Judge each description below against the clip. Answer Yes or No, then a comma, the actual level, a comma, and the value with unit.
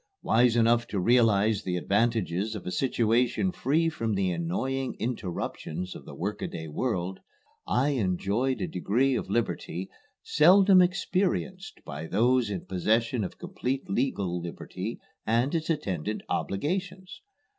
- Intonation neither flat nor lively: No, wide, 5.8 semitones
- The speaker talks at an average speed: No, slow, 130 wpm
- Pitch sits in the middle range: No, low, 115 Hz